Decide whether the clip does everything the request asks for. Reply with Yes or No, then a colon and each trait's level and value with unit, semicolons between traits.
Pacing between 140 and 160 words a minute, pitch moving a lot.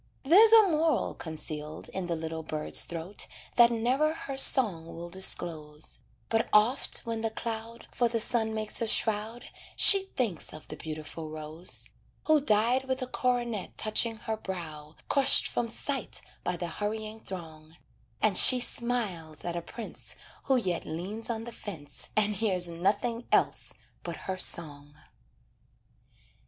Yes: average, 150 wpm; wide, 6.1 semitones